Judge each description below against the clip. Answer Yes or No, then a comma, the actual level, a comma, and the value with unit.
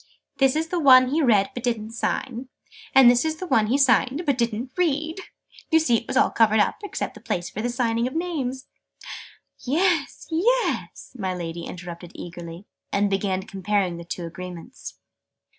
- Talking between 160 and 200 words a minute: Yes, average, 175 wpm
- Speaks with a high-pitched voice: Yes, high, 240 Hz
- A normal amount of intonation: No, wide, 6.4 semitones